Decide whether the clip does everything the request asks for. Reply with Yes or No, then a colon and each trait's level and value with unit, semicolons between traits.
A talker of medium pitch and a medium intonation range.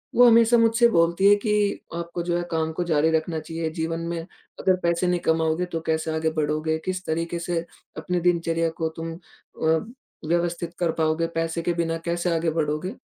No: medium, 170 Hz; narrow, 1.5 semitones